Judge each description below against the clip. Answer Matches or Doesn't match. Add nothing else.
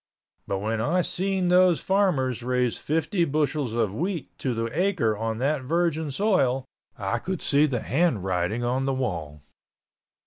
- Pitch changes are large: Matches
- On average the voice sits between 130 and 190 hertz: Matches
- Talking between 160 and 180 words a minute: Doesn't match